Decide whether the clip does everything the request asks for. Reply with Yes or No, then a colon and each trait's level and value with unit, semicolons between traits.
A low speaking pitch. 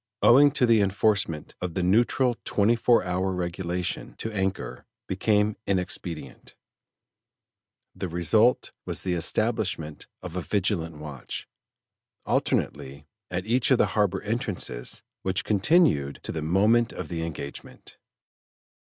Yes: very low, 95 Hz